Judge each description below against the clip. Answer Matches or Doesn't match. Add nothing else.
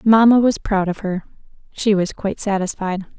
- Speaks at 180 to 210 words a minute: Doesn't match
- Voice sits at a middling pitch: Doesn't match